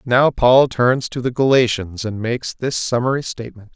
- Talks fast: No, average, 175 wpm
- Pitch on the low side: Yes, low, 120 Hz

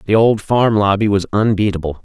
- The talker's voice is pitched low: Yes, low, 105 Hz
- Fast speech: No, average, 175 wpm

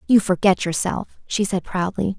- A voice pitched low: No, high, 190 Hz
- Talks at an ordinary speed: Yes, average, 165 wpm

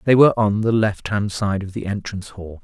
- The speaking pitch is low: Yes, low, 105 Hz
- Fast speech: Yes, fast, 250 wpm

